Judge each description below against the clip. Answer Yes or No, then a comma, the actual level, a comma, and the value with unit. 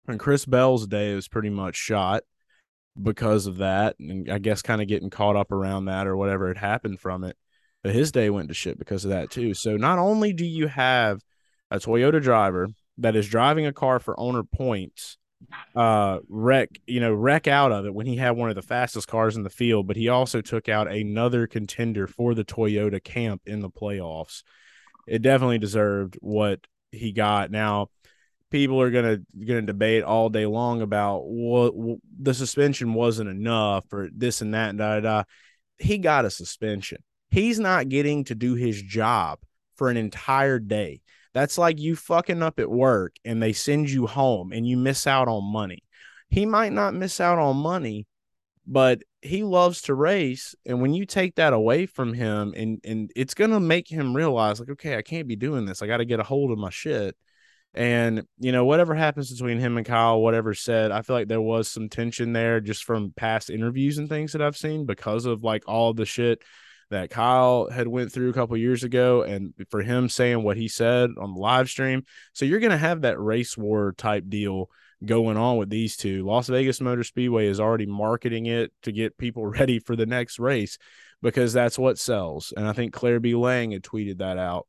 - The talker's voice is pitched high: No, low, 115 Hz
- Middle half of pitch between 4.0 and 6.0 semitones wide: No, average, 3.4 semitones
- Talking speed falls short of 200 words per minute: No, fast, 205 wpm